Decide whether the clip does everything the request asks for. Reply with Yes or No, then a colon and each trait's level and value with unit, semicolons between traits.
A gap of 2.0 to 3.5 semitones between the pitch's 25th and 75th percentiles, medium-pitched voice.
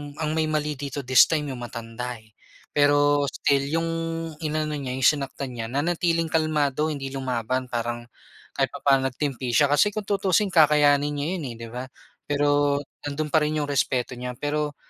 Yes: average, 2.9 semitones; medium, 145 Hz